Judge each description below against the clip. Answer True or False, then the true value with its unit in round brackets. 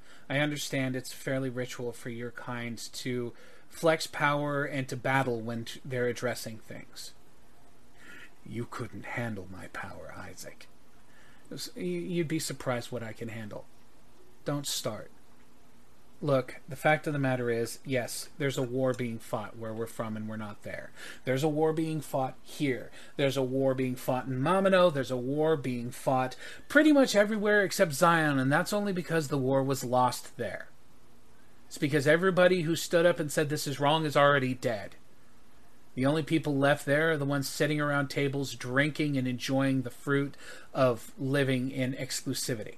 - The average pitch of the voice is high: False (135 Hz)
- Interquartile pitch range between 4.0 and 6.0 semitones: False (3.4 semitones)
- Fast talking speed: False (170 wpm)